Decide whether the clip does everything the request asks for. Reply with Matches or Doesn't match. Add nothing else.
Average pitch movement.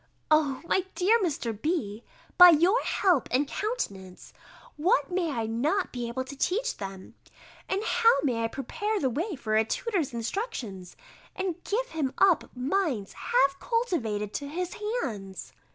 Doesn't match